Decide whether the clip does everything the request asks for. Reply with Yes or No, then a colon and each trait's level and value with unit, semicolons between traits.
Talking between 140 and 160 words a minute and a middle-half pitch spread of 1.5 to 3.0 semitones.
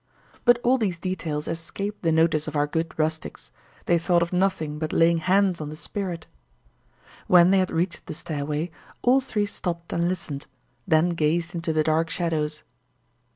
No: average, 170 wpm; average, 2.7 semitones